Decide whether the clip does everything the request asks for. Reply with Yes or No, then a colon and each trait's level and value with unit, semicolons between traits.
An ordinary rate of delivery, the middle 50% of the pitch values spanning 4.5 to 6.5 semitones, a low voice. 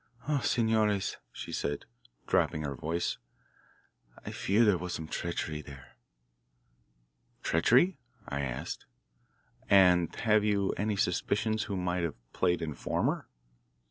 No: slow, 115 wpm; average, 5.0 semitones; very low, 90 Hz